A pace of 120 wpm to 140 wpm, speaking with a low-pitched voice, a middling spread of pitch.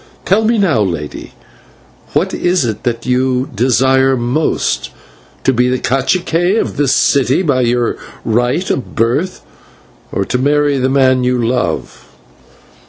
Yes: slow, 135 wpm; low, 130 Hz; average, 3.2 semitones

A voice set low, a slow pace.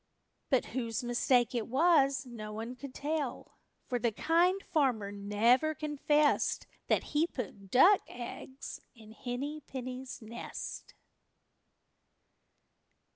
No: very high, 255 Hz; slow, 110 wpm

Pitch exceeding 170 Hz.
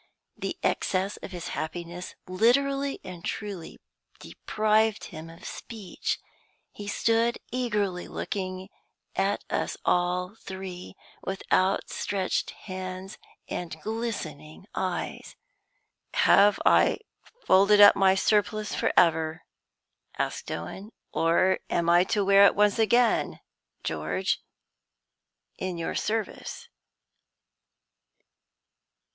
Yes: high, 190 Hz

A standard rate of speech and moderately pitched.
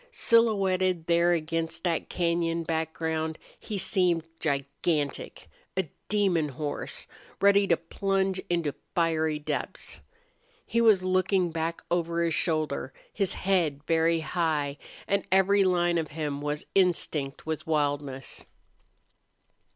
No: slow, 115 wpm; medium, 165 Hz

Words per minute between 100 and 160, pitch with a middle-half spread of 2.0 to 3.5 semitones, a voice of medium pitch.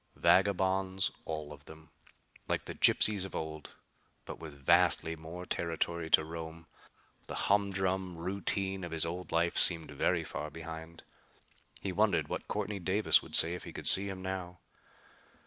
No: average, 155 wpm; average, 2.8 semitones; very low, 85 Hz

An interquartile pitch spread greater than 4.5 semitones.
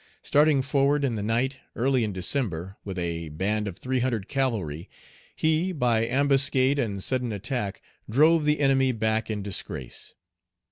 Yes: average, 5.2 semitones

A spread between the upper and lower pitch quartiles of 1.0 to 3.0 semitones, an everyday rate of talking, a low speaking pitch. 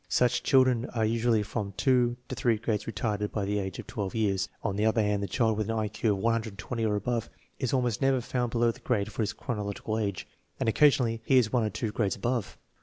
No: narrow, 2.6 semitones; fast, 235 wpm; low, 110 Hz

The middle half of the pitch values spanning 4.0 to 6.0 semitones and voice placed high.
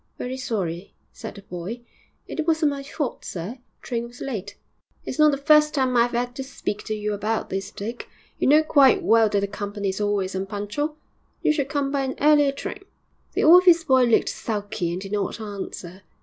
Yes: wide, 5.6 semitones; high, 235 Hz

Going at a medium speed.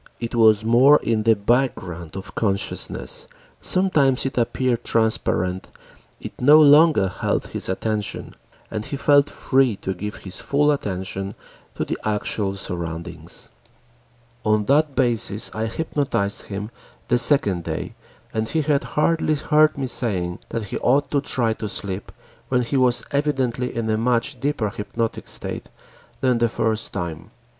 Yes: average, 150 wpm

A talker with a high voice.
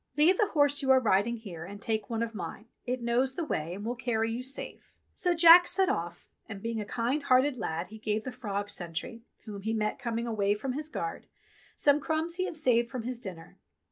Yes: high, 235 Hz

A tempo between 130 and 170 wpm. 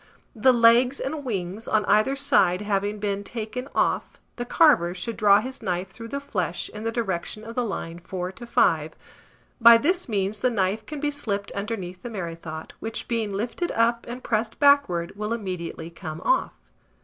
No: average, 180 wpm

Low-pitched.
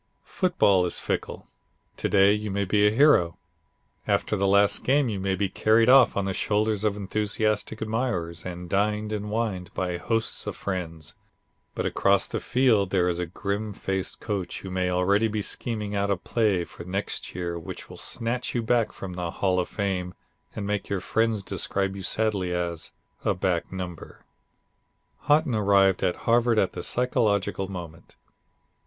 Yes: low, 100 Hz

